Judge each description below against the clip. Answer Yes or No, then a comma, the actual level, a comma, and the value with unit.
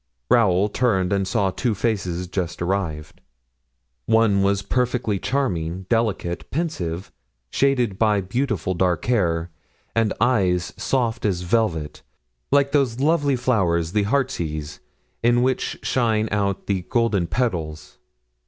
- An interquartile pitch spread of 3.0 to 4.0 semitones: No, average, 5.2 semitones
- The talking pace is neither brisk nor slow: No, slow, 120 wpm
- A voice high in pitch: No, low, 100 Hz